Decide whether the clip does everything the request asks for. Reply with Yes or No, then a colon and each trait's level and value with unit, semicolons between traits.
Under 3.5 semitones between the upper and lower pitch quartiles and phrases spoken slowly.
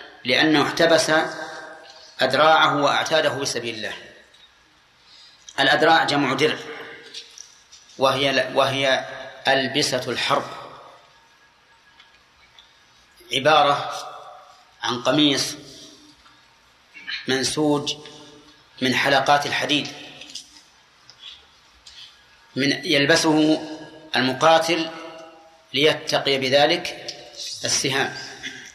Yes: narrow, 2.6 semitones; slow, 55 wpm